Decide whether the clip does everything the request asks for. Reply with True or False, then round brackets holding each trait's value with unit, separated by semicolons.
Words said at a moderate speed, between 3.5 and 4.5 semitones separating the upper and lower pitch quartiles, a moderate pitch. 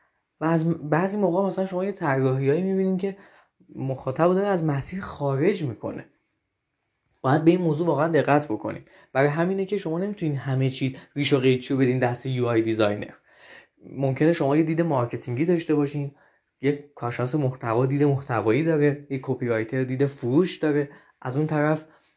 False (160 wpm; 3.9 semitones; 145 Hz)